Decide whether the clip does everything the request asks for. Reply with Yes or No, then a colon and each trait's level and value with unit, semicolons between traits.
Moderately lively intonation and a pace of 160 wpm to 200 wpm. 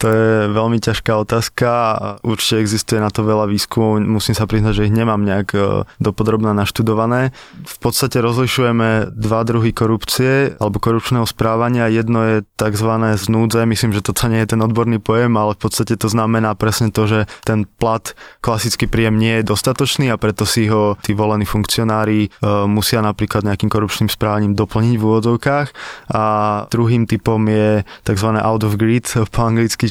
No: narrow, 1.3 semitones; fast, 165 wpm